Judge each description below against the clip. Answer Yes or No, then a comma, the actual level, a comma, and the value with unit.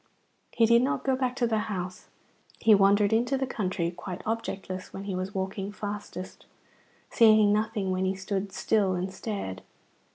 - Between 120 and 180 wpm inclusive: Yes, average, 165 wpm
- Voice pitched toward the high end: Yes, high, 205 Hz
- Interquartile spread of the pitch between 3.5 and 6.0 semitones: No, average, 2.8 semitones